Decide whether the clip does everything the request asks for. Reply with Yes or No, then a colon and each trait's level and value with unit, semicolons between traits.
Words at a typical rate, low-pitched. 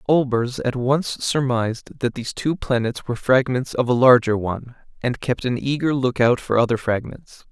Yes: average, 185 wpm; low, 125 Hz